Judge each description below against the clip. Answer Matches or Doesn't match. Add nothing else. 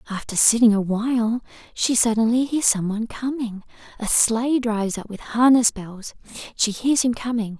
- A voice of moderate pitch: Doesn't match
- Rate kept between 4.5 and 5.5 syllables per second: Matches